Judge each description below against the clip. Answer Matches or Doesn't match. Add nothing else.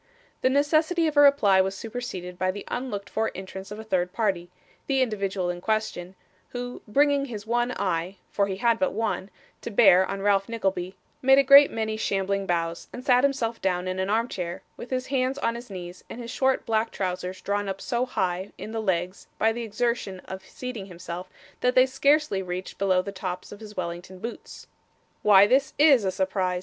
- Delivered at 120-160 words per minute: Doesn't match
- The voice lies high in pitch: Matches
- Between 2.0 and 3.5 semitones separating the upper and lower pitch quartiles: Doesn't match